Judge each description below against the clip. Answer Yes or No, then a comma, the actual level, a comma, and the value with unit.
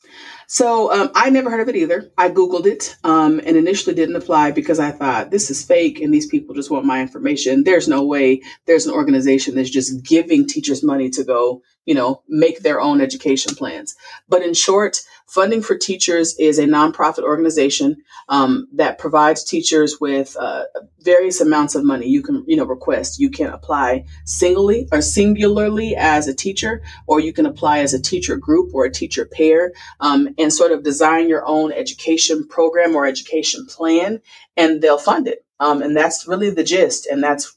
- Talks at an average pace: Yes, average, 190 wpm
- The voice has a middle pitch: Yes, medium, 165 Hz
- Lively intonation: Yes, wide, 6.7 semitones